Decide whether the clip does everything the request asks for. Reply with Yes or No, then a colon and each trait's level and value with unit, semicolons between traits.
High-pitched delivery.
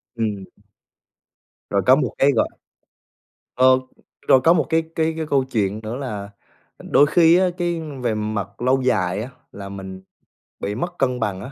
No: low, 125 Hz